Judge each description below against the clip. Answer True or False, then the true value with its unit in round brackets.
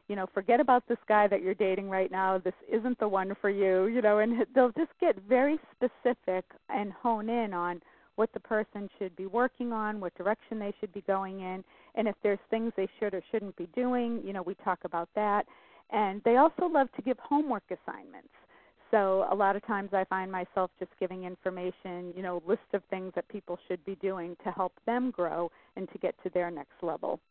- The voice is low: False (200 Hz)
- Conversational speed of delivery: False (220 wpm)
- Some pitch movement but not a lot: True (3.5 semitones)